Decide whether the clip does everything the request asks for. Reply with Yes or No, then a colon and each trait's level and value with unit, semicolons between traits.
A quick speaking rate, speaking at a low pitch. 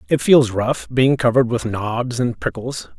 No: average, 180 wpm; low, 120 Hz